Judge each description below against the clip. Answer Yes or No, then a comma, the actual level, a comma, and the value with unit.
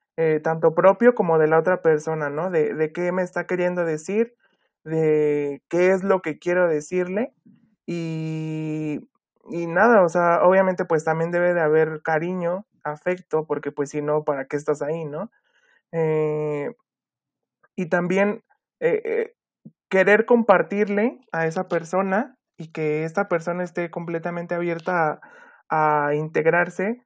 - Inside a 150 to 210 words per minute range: No, average, 140 wpm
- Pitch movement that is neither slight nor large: Yes, average, 3.4 semitones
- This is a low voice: No, medium, 170 Hz